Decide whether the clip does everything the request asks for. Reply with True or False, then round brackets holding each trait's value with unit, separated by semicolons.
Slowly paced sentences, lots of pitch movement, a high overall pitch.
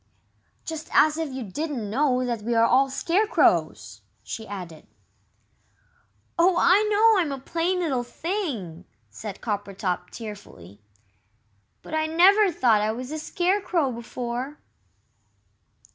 True (125 wpm; 7.4 semitones; 265 Hz)